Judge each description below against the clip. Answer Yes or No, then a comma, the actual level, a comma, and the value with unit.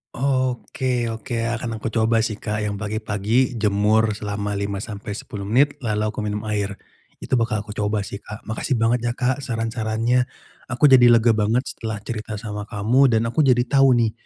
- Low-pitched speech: Yes, low, 110 Hz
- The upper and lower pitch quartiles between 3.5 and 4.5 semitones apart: No, average, 2.7 semitones